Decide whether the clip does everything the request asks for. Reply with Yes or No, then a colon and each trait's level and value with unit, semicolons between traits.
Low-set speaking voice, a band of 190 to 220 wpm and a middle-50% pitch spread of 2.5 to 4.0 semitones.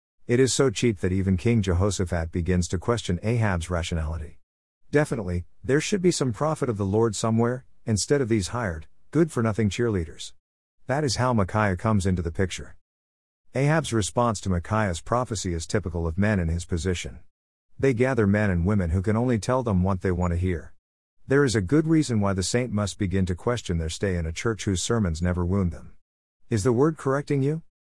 No: low, 100 Hz; average, 200 wpm; wide, 5.4 semitones